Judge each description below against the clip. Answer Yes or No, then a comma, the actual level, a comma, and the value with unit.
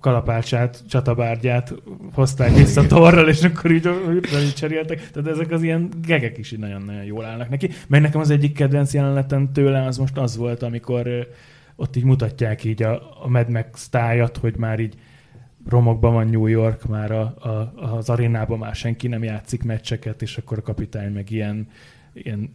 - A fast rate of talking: Yes, fast, 175 wpm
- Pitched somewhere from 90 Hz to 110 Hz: No, low, 120 Hz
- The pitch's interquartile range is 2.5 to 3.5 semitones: No, average, 4.0 semitones